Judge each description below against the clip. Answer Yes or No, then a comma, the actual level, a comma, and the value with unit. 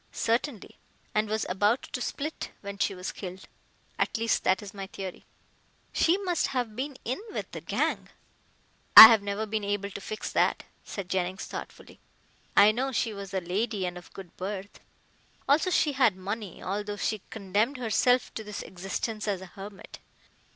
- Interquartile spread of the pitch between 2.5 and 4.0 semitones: Yes, average, 3.1 semitones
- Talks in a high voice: Yes, high, 205 Hz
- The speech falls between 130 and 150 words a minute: No, average, 170 wpm